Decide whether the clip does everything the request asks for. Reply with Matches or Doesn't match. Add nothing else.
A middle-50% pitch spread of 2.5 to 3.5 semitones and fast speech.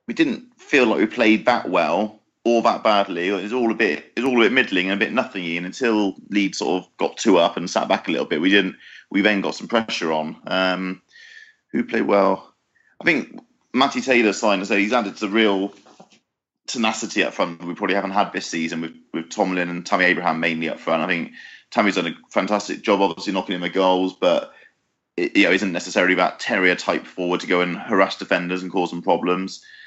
Matches